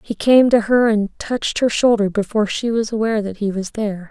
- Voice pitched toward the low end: No, high, 215 Hz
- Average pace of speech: No, fast, 235 wpm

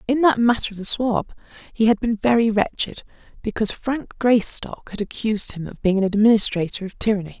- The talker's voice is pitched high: Yes, high, 215 Hz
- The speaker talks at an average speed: Yes, average, 185 wpm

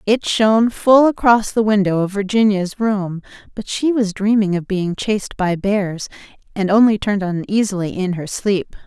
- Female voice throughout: Yes, female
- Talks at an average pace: Yes, average, 170 wpm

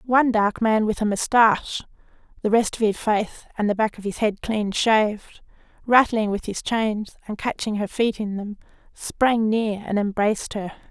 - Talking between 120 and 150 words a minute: No, average, 185 wpm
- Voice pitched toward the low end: No, high, 215 Hz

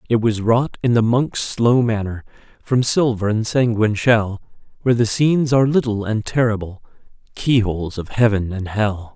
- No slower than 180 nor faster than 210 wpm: No, average, 165 wpm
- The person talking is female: No, male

